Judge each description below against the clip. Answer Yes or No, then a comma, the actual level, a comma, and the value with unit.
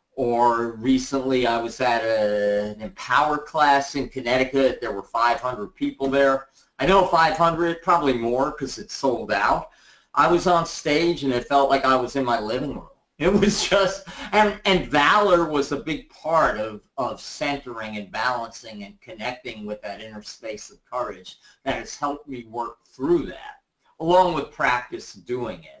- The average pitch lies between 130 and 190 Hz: Yes, low, 135 Hz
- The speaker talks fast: No, average, 170 wpm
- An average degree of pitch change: No, wide, 5.9 semitones